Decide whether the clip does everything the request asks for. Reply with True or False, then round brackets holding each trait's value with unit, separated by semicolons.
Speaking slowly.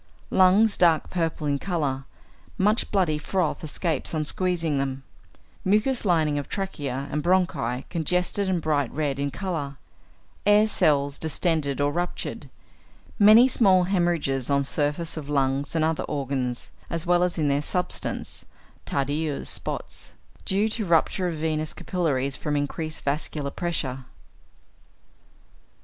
True (130 wpm)